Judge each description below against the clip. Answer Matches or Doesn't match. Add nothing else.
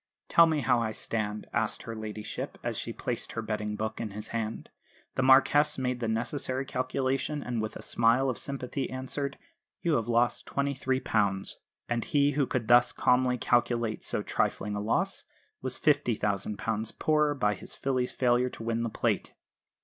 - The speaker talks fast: Doesn't match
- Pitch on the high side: Doesn't match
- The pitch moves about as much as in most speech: Matches